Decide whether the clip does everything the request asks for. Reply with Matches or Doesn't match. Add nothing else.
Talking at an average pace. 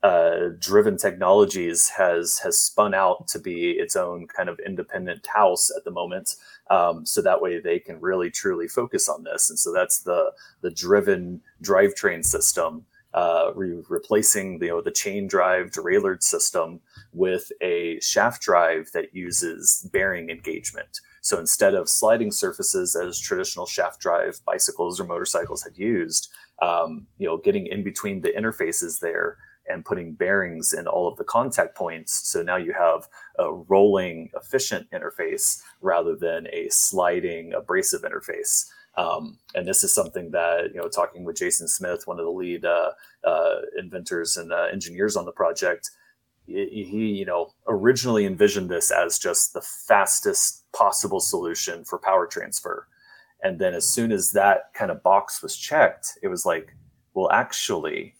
Matches